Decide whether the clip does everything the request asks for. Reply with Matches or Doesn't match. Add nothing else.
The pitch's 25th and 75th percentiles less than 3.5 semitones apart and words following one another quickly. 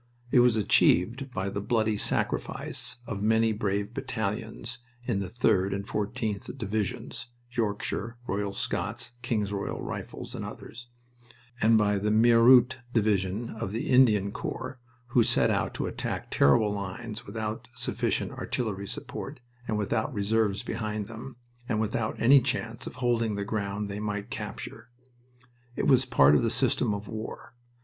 Doesn't match